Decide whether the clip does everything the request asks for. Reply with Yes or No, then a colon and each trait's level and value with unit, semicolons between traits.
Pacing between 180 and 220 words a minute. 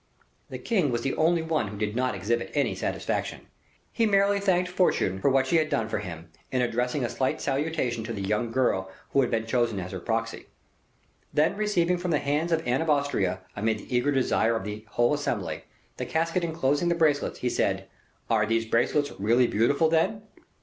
Yes: average, 200 wpm